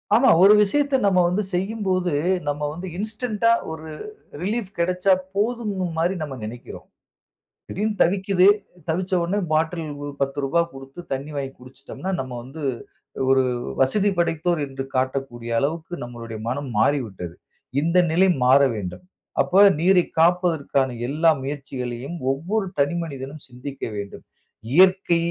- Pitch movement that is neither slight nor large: No, wide, 5.8 semitones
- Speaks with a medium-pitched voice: Yes, medium, 160 Hz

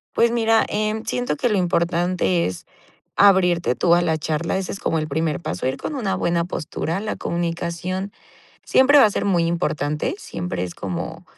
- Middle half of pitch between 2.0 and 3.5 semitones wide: No, average, 3.9 semitones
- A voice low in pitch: No, medium, 175 Hz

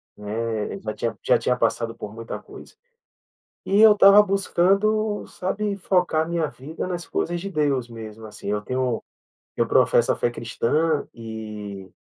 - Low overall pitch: Yes, low, 130 Hz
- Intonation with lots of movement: Yes, wide, 8.7 semitones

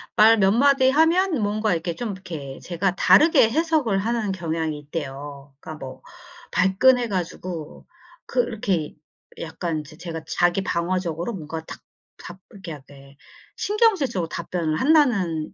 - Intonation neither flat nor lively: No, wide, 6.4 semitones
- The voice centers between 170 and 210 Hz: Yes, medium, 185 Hz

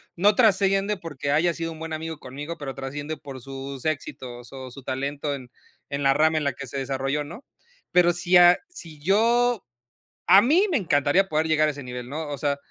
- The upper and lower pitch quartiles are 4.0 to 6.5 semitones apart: Yes, average, 4.3 semitones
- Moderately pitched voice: Yes, medium, 150 Hz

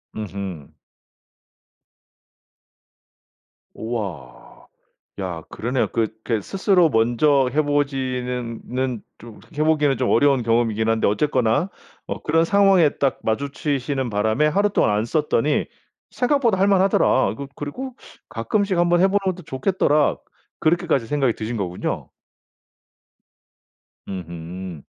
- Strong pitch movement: Yes, wide, 6.1 semitones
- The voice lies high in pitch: No, low, 130 Hz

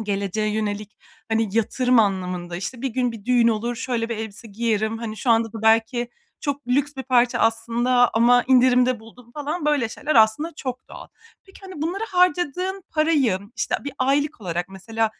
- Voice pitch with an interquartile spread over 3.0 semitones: Yes, average, 3.5 semitones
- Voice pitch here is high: Yes, high, 235 Hz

